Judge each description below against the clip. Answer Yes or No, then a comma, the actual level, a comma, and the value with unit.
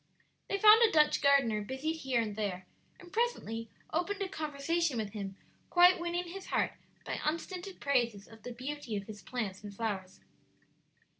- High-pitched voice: Yes, very high, 275 Hz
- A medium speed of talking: Yes, average, 165 wpm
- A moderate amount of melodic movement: No, wide, 8.1 semitones